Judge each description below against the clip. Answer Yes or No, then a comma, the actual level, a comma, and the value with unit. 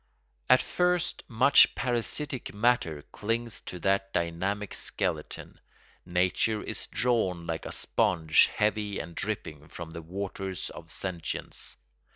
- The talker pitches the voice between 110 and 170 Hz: No, very low, 95 Hz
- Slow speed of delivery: Yes, slow, 120 wpm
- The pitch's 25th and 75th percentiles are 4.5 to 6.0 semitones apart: Yes, average, 5.2 semitones